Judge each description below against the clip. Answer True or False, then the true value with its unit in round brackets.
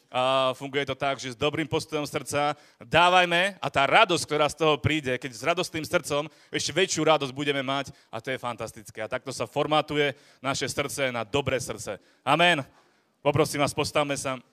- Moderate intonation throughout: False (2.3 semitones)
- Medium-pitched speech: True (145 Hz)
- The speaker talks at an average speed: False (180 wpm)